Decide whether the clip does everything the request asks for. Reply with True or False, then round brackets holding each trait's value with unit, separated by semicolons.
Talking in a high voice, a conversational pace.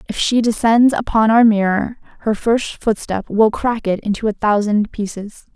True (215 Hz; 175 wpm)